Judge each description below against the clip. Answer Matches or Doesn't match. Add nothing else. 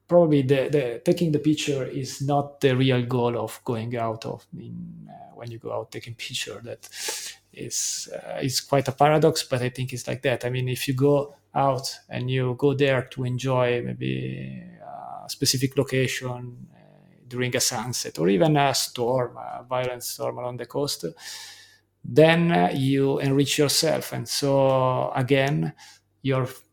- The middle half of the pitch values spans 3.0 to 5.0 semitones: Doesn't match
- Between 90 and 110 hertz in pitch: Doesn't match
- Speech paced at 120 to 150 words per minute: Doesn't match